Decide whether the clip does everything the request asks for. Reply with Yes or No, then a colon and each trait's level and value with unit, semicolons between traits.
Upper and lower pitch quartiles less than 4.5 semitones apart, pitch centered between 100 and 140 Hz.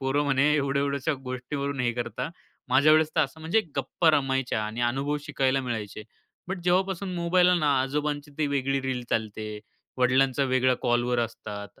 Yes: average, 3.1 semitones; low, 135 Hz